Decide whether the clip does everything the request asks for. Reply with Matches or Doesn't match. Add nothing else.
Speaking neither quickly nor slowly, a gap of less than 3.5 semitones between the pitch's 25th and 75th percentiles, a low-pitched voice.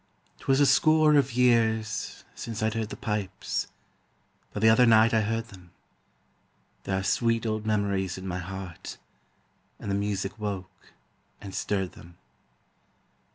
Matches